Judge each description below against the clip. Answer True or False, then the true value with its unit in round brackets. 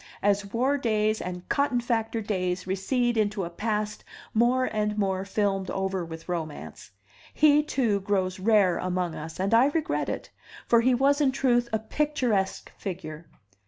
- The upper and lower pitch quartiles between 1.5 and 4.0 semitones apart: False (4.5 semitones)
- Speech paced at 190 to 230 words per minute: False (160 wpm)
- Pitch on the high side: True (210 Hz)